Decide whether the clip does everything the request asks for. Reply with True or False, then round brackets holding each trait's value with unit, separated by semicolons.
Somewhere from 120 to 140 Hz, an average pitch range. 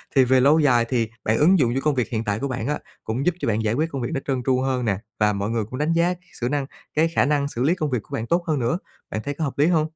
True (135 Hz; 4.5 semitones)